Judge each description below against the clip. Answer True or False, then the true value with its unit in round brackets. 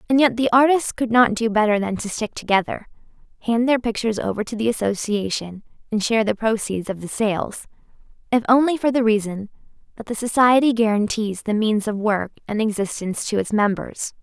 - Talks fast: False (185 wpm)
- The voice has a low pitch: False (220 Hz)